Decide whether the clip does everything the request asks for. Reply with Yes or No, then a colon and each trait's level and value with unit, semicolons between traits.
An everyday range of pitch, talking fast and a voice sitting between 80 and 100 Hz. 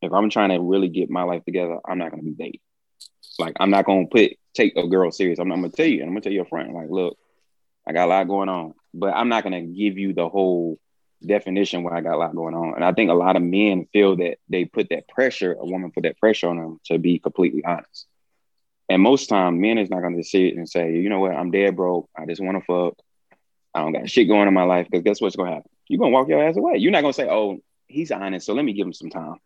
No: narrow, 2.2 semitones; fast, 295 wpm; very low, 90 Hz